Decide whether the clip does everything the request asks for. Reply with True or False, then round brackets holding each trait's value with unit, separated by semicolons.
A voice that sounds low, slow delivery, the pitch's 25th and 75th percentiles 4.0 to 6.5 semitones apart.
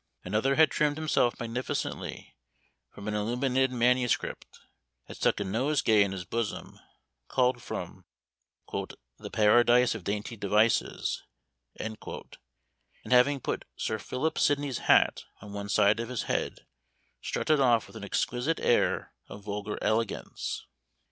False (115 Hz; 130 wpm; 3.4 semitones)